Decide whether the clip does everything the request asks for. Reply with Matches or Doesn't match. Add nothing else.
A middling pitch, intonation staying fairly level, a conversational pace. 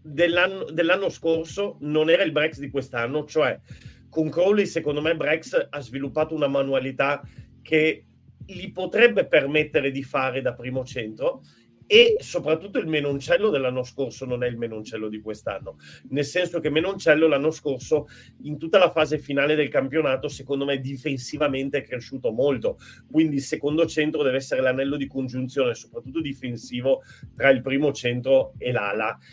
Doesn't match